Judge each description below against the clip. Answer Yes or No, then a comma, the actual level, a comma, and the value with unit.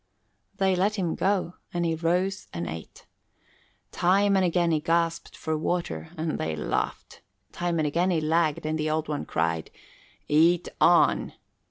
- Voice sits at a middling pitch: Yes, medium, 165 Hz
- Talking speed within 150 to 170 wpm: Yes, average, 160 wpm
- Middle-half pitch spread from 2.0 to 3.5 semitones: Yes, narrow, 2.6 semitones